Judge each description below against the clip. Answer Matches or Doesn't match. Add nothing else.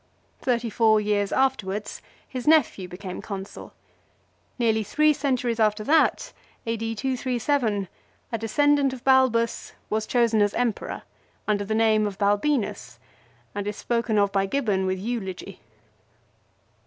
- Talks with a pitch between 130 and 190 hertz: Doesn't match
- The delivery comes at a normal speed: Doesn't match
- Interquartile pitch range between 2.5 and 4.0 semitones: Matches